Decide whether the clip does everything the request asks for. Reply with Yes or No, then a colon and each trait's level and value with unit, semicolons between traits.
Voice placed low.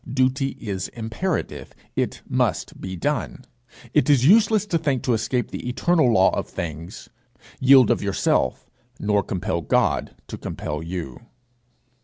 Yes: low, 120 Hz